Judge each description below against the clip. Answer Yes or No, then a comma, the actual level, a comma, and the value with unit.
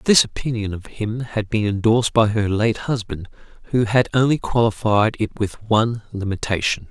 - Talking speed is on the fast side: No, average, 165 wpm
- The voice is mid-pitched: No, low, 110 Hz